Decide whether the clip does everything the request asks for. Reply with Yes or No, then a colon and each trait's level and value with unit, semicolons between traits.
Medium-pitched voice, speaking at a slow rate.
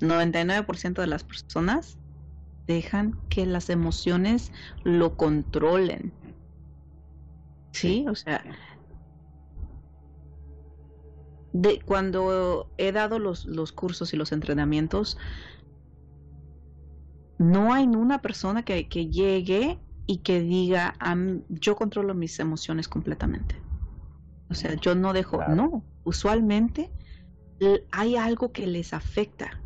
Yes: medium, 165 Hz; slow, 105 wpm